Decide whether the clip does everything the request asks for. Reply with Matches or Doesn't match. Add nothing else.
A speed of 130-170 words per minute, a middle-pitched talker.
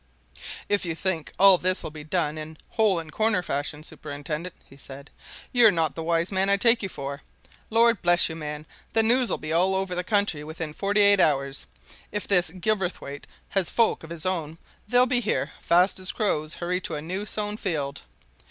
Doesn't match